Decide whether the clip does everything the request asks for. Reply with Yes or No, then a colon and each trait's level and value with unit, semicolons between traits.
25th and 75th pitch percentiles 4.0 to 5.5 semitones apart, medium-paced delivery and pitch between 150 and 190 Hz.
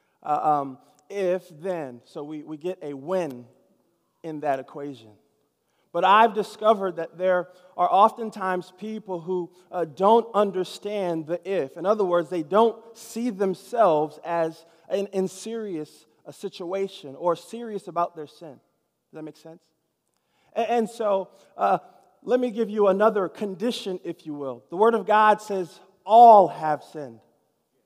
Yes: average, 4.5 semitones; average, 150 wpm; medium, 185 Hz